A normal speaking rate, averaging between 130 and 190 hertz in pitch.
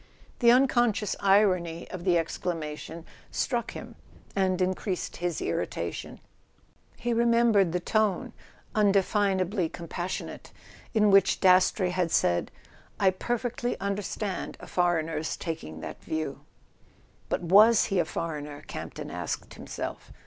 No: slow, 115 wpm; medium, 185 Hz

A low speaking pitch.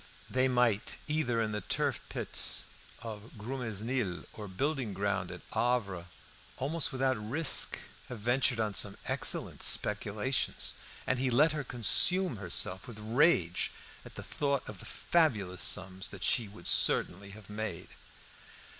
Yes: low, 110 Hz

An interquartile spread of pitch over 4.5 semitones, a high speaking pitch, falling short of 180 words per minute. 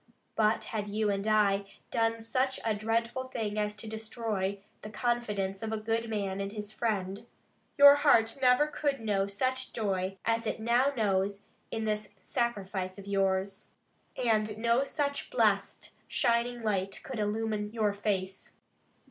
No: narrow, 2.6 semitones; high, 215 Hz; average, 150 wpm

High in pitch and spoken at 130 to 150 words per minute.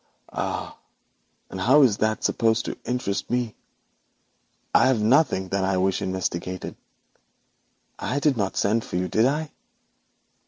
No: low, 110 Hz; slow, 135 wpm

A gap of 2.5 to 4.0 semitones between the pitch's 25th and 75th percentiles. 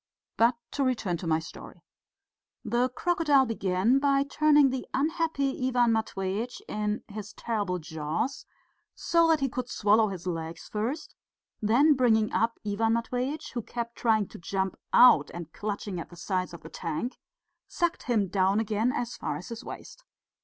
No: average, 4.9 semitones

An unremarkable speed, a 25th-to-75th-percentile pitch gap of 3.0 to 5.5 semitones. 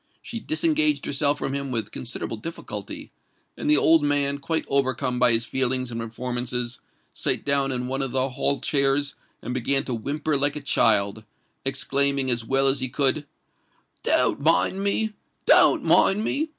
No: average, 160 wpm; narrow, 2.6 semitones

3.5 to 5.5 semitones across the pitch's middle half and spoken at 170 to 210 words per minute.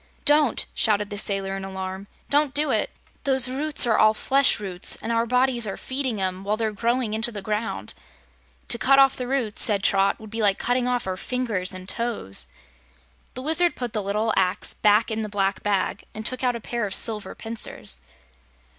Yes: average, 4.0 semitones; average, 200 wpm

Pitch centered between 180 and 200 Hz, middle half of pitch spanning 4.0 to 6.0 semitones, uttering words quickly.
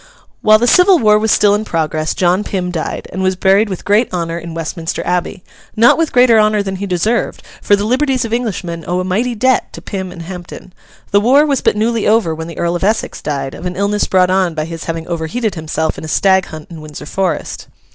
Yes: high, 190 Hz; average, 4.3 semitones; fast, 225 wpm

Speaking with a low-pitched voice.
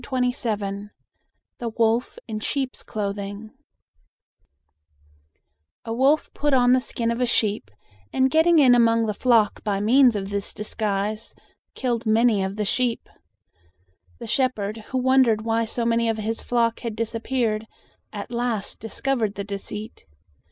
No: high, 230 Hz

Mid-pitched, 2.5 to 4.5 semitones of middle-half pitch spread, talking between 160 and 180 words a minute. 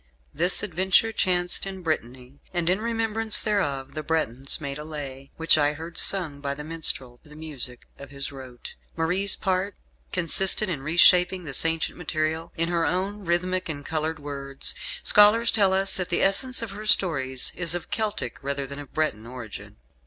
No: medium, 165 Hz; average, 5.1 semitones; average, 175 wpm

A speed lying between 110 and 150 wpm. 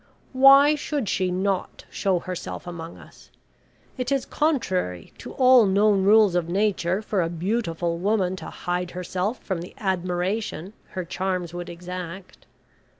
Yes: average, 145 wpm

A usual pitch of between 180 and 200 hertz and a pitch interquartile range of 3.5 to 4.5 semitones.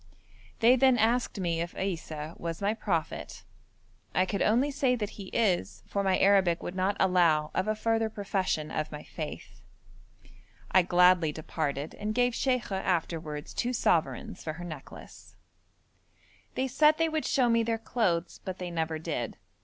No: high, 190 Hz; wide, 5.4 semitones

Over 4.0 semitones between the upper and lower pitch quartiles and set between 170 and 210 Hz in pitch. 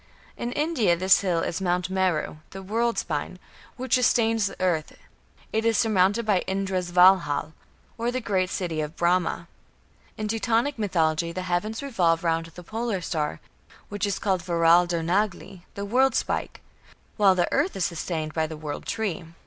Yes: average, 4.4 semitones; medium, 185 Hz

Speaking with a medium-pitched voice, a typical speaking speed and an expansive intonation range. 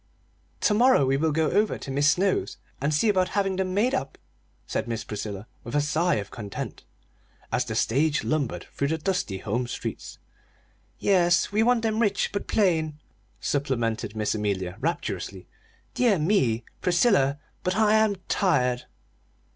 Yes: medium, 155 Hz; average, 155 wpm; wide, 8.3 semitones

